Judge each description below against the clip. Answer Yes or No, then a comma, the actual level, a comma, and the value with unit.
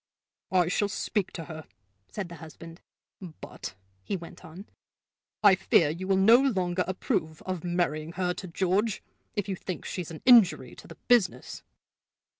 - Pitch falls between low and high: Yes, medium, 180 Hz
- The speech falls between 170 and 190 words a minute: No, average, 160 wpm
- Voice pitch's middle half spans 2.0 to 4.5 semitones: Yes, average, 2.8 semitones